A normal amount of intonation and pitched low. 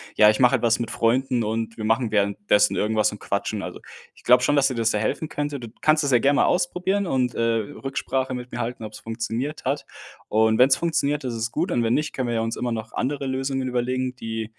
Yes: average, 3.1 semitones; low, 125 Hz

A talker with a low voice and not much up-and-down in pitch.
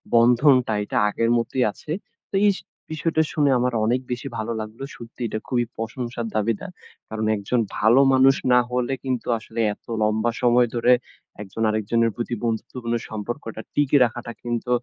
Yes: low, 120 Hz; narrow, 2.2 semitones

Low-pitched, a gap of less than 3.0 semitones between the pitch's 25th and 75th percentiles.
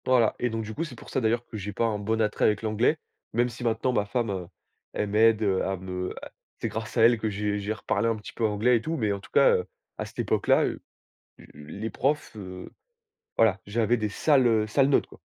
Yes: low, 110 Hz; narrow, 2.4 semitones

